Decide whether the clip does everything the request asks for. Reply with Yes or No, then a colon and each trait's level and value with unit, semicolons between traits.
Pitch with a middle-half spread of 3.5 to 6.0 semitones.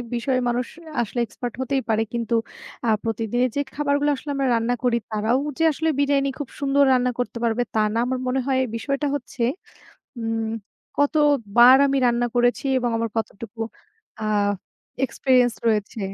No: average, 3.0 semitones